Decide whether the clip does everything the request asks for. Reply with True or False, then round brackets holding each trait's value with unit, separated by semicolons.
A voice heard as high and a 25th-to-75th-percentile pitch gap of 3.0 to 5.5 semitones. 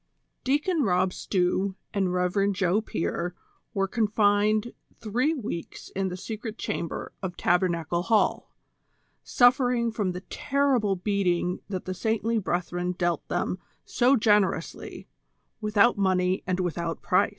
True (195 Hz; 3.6 semitones)